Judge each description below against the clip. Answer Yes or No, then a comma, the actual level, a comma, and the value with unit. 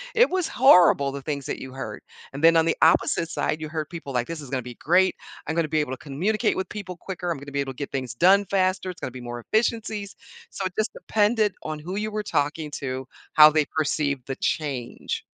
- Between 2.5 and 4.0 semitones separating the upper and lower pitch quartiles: No, average, 5.3 semitones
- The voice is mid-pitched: Yes, medium, 155 Hz